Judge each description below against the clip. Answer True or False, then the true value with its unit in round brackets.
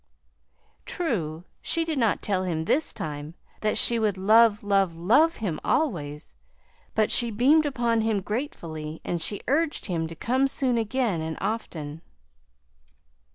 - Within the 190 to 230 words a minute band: False (145 wpm)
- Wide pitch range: True (7.0 semitones)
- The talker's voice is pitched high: True (210 Hz)